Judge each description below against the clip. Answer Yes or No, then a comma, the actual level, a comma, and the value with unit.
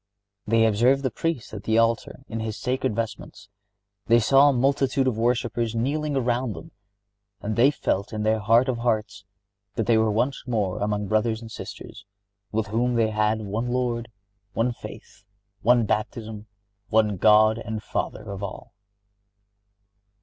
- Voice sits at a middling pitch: No, low, 115 Hz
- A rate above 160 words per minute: No, average, 155 wpm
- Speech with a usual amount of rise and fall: No, narrow, 2.3 semitones